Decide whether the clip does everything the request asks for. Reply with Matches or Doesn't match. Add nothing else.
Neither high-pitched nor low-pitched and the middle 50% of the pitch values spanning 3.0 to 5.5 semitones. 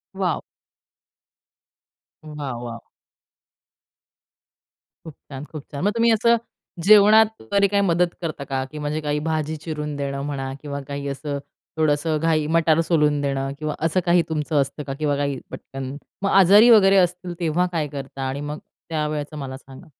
Matches